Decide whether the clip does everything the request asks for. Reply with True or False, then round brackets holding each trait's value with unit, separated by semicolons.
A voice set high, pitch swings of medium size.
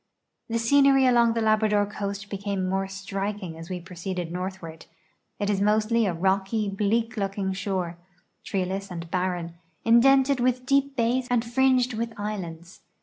True (205 Hz; 3.7 semitones)